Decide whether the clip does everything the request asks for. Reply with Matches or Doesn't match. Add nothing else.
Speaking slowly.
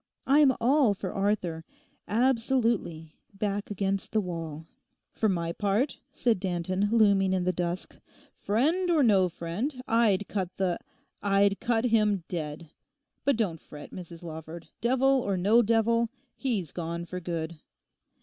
Matches